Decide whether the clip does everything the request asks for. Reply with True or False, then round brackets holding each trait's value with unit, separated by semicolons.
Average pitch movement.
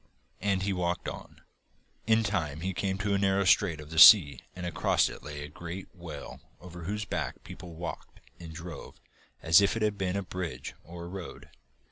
True (3.0 semitones)